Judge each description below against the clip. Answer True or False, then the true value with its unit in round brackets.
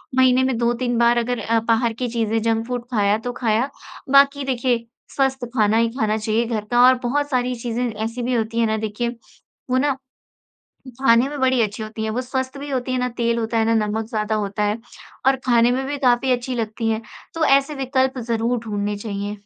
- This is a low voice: False (235 Hz)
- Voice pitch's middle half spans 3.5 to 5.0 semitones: False (2.6 semitones)